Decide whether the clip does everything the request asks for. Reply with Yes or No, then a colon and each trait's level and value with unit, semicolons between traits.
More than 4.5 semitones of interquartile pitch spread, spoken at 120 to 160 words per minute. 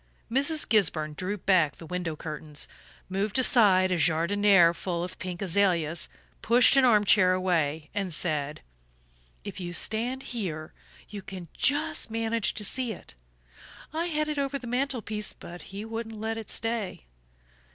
Yes: average, 4.9 semitones; average, 155 wpm